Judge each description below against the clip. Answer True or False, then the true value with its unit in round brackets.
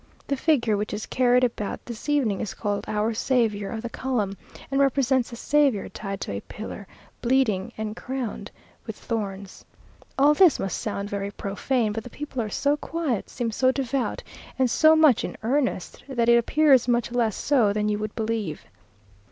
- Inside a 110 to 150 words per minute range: False (180 wpm)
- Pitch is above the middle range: True (235 Hz)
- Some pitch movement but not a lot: True (4.1 semitones)